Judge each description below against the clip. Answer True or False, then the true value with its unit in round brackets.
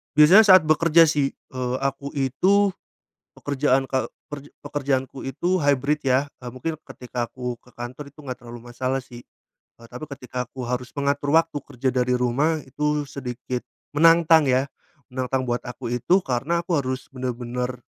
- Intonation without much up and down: False (3.1 semitones)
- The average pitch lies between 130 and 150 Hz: True (135 Hz)